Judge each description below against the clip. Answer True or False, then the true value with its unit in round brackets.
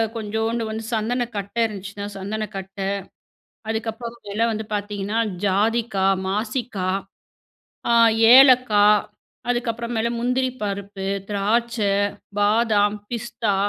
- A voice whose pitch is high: True (220 Hz)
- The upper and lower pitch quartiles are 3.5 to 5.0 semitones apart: False (2.5 semitones)